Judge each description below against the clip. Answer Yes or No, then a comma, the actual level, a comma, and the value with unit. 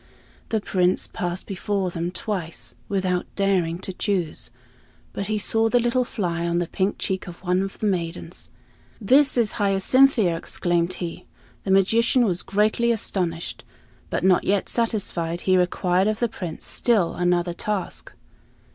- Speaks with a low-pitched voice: No, high, 190 Hz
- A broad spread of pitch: No, average, 3.3 semitones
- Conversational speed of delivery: Yes, average, 150 wpm